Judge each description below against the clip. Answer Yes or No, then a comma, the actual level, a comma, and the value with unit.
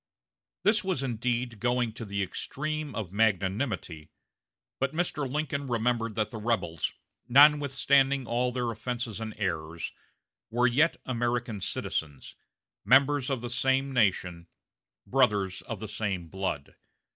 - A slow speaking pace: Yes, slow, 125 wpm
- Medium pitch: No, low, 120 Hz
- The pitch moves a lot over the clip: No, average, 4.9 semitones